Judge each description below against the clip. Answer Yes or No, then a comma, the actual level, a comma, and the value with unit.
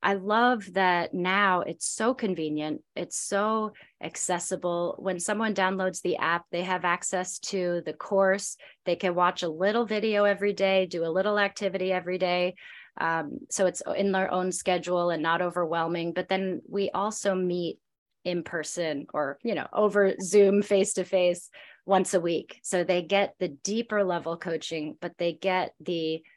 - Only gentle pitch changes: Yes, narrow, 2.3 semitones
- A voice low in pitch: No, medium, 185 Hz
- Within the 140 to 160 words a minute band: No, average, 170 wpm